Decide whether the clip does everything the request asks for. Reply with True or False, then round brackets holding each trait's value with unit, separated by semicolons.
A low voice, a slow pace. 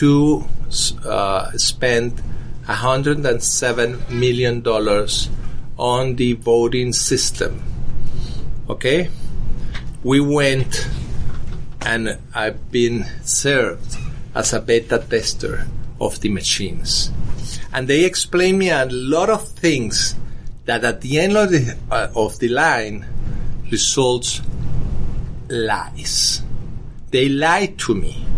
True (125 Hz; 100 wpm)